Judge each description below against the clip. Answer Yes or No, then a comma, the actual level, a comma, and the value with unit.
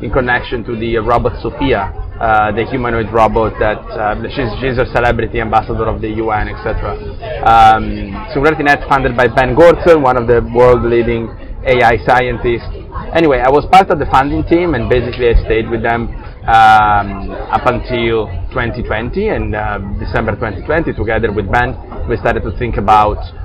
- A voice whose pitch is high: No, low, 115 Hz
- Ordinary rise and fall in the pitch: No, narrow, 2.3 semitones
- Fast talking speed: No, average, 165 wpm